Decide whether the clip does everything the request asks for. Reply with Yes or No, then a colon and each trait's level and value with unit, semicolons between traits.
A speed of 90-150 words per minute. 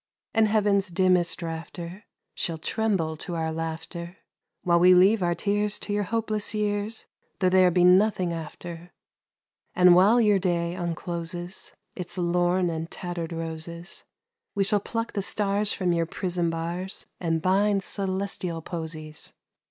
Yes: average, 140 wpm